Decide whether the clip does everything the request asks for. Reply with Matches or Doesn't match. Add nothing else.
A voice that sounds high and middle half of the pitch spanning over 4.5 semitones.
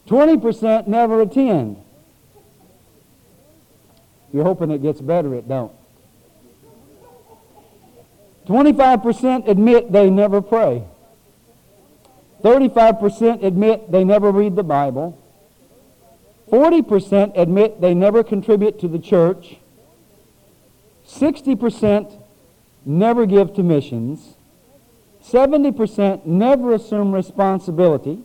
Matches